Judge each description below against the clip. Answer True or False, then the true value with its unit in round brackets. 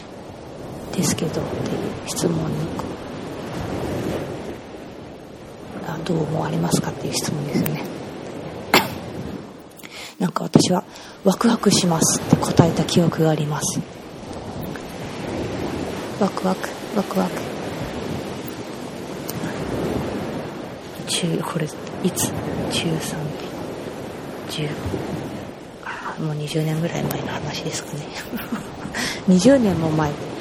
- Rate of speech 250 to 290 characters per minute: False (155 characters per minute)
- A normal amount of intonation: True (3.8 semitones)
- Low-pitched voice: False (165 Hz)